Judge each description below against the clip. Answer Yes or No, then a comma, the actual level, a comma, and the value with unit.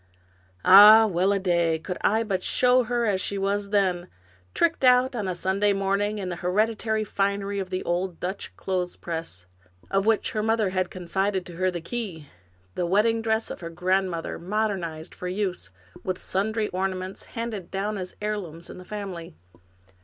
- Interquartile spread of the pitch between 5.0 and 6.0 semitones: No, average, 2.8 semitones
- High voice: Yes, high, 195 Hz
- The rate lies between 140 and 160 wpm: No, average, 175 wpm